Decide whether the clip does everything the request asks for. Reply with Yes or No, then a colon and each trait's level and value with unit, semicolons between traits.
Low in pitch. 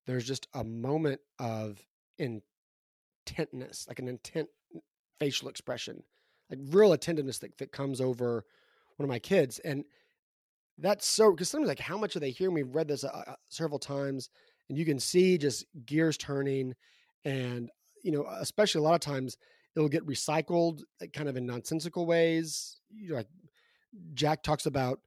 No: medium, 145 Hz